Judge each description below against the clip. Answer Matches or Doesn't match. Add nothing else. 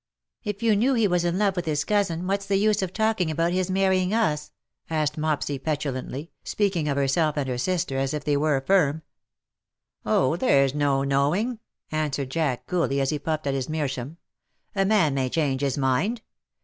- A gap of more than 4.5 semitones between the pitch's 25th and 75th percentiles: Matches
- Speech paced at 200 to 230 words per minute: Matches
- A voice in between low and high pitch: Matches